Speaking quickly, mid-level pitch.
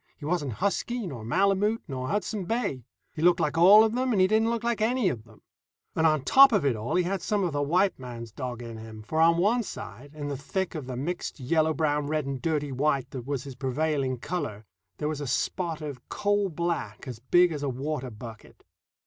Yes: fast, 225 wpm; medium, 155 Hz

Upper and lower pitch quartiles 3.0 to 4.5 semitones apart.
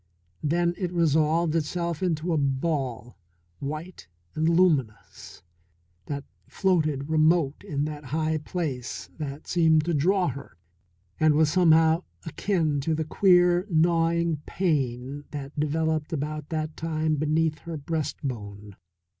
No: narrow, 2.6 semitones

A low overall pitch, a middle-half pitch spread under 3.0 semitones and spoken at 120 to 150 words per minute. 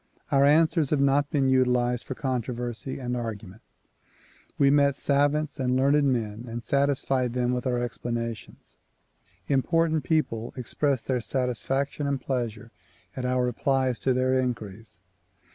Yes: low, 130 Hz; narrow, 2.4 semitones; slow, 135 wpm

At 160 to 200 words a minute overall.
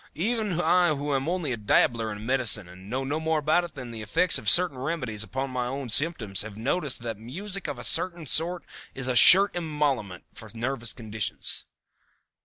Yes: average, 195 wpm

